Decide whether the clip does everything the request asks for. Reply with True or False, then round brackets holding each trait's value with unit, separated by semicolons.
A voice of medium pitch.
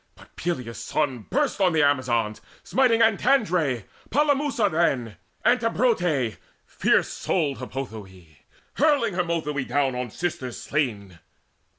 True (150 Hz)